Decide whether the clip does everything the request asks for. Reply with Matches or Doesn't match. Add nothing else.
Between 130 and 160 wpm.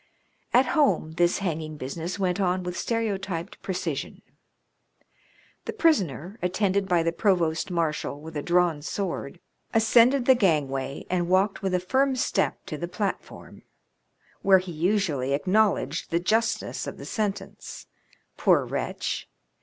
Matches